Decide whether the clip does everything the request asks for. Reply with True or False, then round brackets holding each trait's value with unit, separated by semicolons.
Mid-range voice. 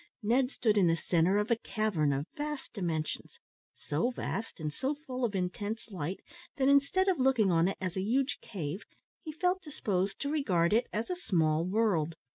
False (210 Hz)